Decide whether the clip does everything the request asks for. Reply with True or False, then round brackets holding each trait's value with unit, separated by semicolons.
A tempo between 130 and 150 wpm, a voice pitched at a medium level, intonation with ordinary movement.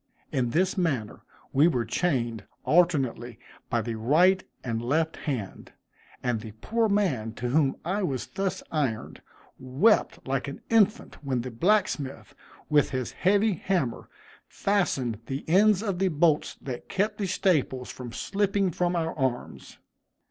False (145 wpm; 150 Hz; 7.3 semitones)